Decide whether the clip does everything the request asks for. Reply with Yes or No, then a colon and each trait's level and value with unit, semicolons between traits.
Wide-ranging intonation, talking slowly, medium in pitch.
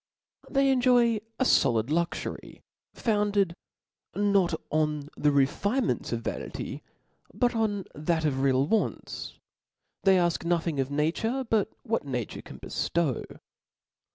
Yes: wide, 7.0 semitones; slow, 120 wpm; medium, 175 Hz